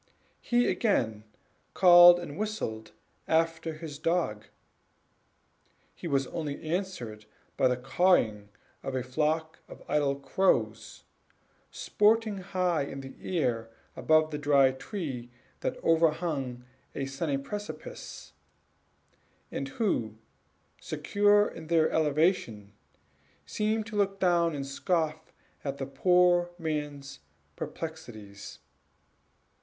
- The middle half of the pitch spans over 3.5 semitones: Yes, average, 4.9 semitones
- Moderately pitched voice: Yes, medium, 155 Hz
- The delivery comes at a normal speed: No, slow, 105 wpm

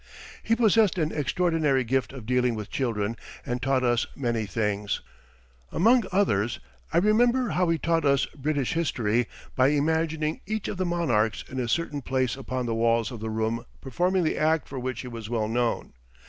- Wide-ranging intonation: Yes, wide, 6.1 semitones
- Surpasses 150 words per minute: Yes, average, 180 wpm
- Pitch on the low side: Yes, low, 130 Hz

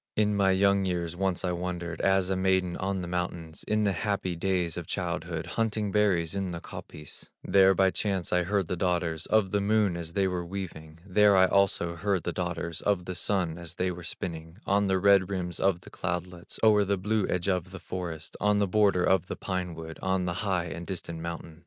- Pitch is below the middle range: Yes, very low, 90 Hz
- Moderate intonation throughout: No, narrow, 2.3 semitones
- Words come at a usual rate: No, fast, 215 wpm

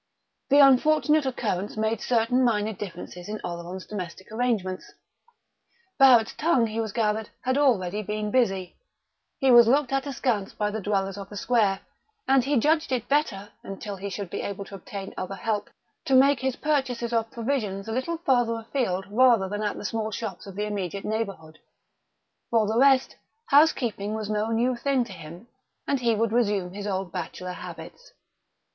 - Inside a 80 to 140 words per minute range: No, average, 170 wpm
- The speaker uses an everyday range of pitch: Yes, average, 4.3 semitones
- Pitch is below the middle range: No, high, 220 Hz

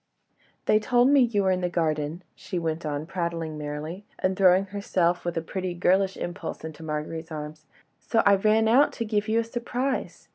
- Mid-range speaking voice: Yes, medium, 180 Hz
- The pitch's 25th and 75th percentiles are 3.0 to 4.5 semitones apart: No, average, 4.9 semitones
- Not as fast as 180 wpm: No, average, 185 wpm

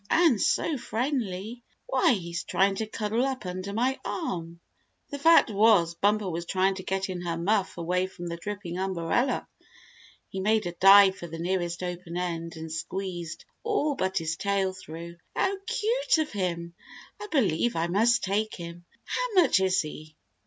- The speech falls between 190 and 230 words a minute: No, average, 170 wpm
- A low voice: No, high, 190 Hz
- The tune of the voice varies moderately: Yes, average, 4.4 semitones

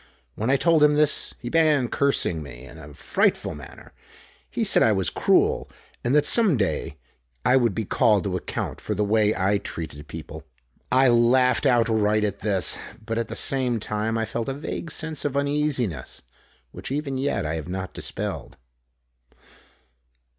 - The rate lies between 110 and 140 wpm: No, average, 170 wpm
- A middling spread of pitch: No, wide, 6.0 semitones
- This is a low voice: Yes, low, 115 Hz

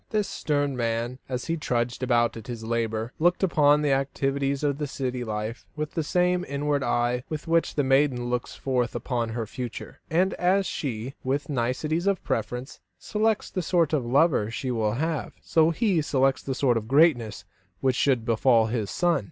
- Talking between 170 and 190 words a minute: Yes, average, 180 wpm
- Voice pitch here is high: No, low, 135 Hz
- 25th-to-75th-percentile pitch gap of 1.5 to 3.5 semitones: No, average, 4.5 semitones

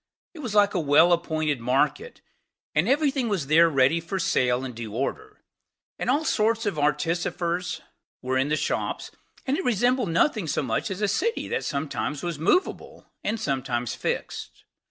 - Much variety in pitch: Yes, wide, 8.3 semitones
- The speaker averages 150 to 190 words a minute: Yes, average, 175 wpm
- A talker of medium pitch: Yes, medium, 170 Hz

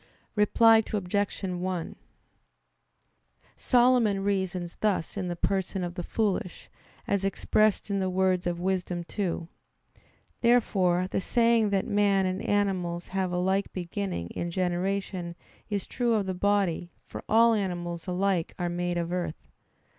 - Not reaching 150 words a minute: Yes, average, 140 wpm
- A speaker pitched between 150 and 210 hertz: Yes, high, 190 Hz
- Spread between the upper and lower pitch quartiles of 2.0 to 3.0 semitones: Yes, narrow, 2.4 semitones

